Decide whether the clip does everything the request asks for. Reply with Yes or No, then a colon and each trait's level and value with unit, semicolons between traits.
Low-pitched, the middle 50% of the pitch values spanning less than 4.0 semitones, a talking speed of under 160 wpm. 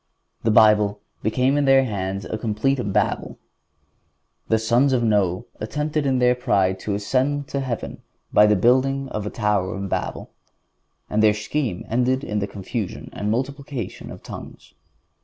No: low, 110 Hz; average, 4.3 semitones; average, 150 wpm